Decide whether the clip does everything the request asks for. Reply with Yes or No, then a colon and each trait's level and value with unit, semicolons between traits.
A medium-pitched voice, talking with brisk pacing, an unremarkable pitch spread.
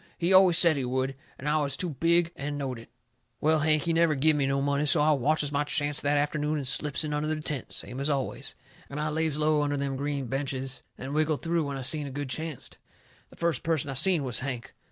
No: medium, 145 Hz; fast, 255 wpm; narrow, 2.2 semitones